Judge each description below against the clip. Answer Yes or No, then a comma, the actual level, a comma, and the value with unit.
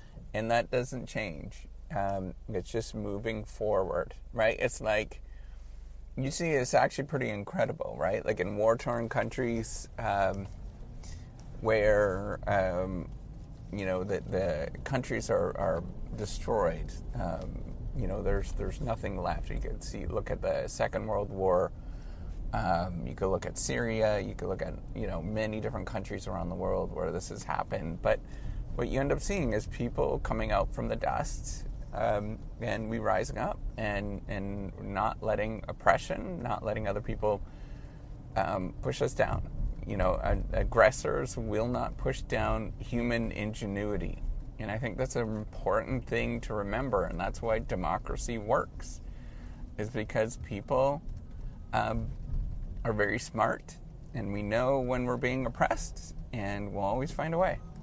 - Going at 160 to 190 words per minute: No, average, 150 wpm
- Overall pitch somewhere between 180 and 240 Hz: No, low, 105 Hz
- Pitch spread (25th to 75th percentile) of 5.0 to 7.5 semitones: No, average, 3.3 semitones